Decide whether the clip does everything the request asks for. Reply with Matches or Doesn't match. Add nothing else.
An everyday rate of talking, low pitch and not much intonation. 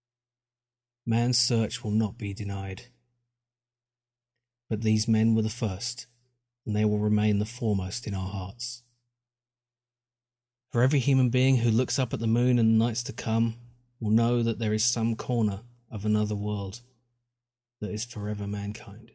Matches